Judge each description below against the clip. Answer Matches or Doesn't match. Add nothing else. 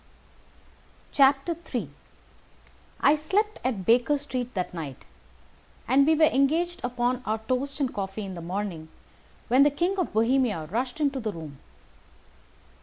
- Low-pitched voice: Doesn't match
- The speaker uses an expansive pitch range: Matches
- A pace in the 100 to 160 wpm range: Matches